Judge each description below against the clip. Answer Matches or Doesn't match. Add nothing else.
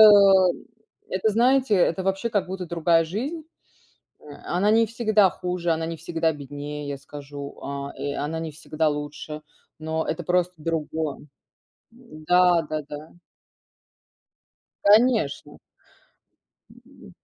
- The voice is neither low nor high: Matches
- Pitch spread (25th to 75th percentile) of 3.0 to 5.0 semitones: Matches